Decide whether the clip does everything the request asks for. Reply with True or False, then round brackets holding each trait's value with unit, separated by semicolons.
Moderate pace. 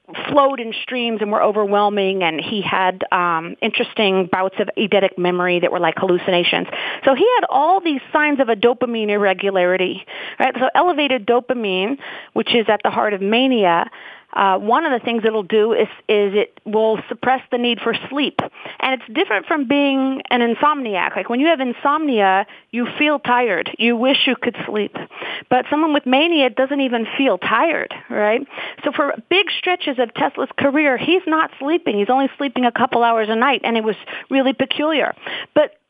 True (180 wpm)